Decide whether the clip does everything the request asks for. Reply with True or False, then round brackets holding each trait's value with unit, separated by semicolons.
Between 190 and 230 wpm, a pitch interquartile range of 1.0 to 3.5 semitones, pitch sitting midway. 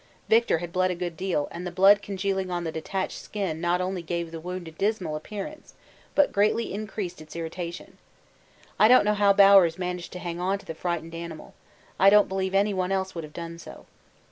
True (205 wpm; 2.7 semitones; 180 Hz)